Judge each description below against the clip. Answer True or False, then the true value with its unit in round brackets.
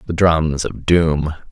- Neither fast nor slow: True (160 wpm)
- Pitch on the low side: True (80 Hz)